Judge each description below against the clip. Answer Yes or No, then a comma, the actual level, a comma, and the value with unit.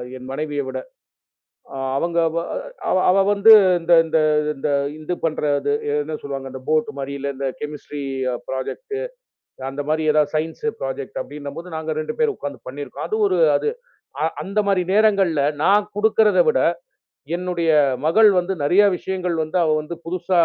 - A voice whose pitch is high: No, medium, 160 Hz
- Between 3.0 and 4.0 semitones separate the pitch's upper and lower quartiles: No, average, 4.6 semitones